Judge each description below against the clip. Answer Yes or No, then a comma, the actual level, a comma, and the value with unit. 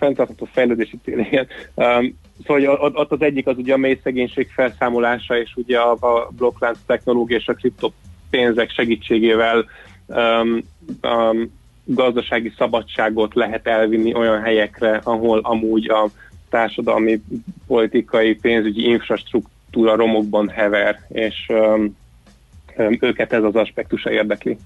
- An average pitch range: No, narrow, 1.7 semitones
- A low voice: Yes, low, 115 Hz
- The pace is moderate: Yes, average, 120 wpm